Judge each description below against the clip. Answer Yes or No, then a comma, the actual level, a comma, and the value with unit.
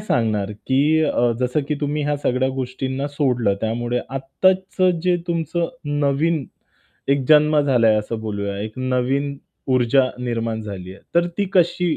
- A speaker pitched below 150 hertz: Yes, low, 135 Hz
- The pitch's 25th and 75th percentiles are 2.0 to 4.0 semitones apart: No, average, 4.7 semitones